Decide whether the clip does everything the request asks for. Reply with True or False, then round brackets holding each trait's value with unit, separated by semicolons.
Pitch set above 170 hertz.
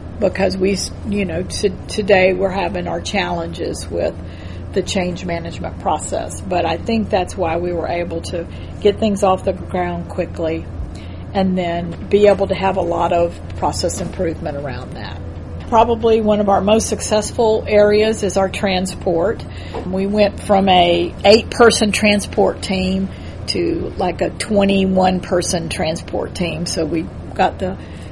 True (190 Hz)